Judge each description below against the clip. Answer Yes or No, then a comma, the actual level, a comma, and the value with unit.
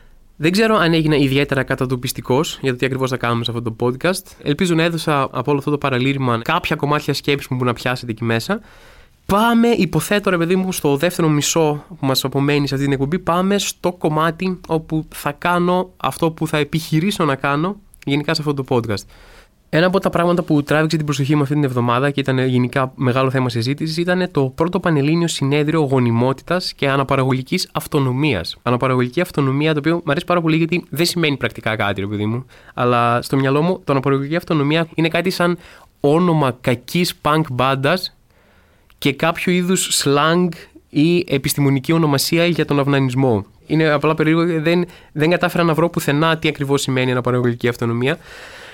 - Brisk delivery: Yes, fast, 180 wpm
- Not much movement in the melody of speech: No, average, 4.2 semitones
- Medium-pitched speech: Yes, medium, 150 Hz